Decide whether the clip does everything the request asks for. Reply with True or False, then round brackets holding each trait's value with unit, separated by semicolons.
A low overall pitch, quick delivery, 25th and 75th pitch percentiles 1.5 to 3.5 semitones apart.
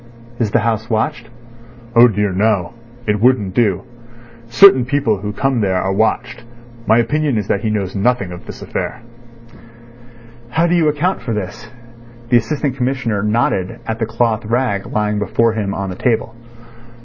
False (110 Hz; 165 wpm; 3.2 semitones)